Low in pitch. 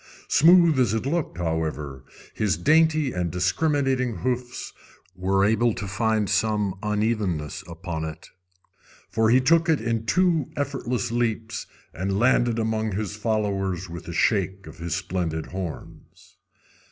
Yes: low, 110 Hz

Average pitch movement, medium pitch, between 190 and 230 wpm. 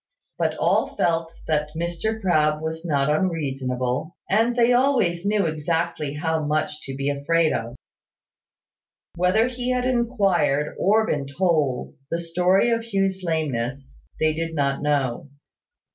No: average, 4.8 semitones; medium, 165 Hz; slow, 135 wpm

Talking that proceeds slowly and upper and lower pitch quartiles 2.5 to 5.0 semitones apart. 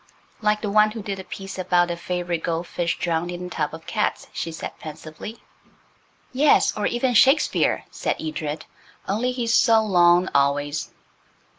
No: average, 165 wpm; average, 4.6 semitones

